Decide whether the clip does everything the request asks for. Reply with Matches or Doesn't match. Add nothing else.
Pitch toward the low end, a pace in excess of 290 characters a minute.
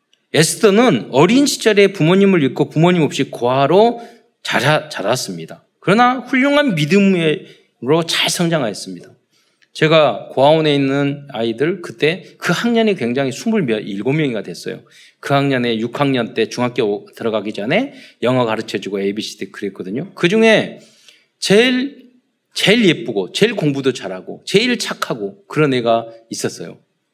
Doesn't match